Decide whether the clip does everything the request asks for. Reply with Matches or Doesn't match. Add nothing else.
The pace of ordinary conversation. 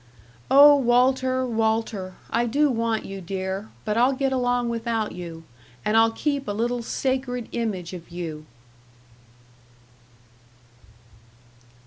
Doesn't match